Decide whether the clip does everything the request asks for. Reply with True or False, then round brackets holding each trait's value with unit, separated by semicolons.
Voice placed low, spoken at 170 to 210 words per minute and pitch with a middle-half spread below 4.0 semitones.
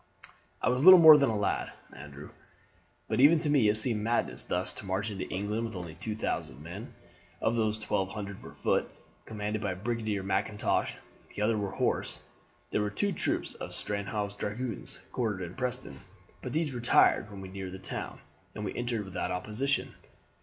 True (105 Hz; 180 wpm; 3.5 semitones)